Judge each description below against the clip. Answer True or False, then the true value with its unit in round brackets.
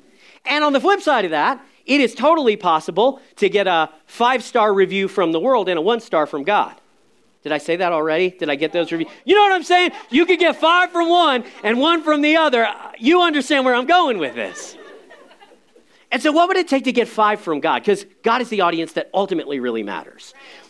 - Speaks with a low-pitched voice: False (245 Hz)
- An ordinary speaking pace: False (230 wpm)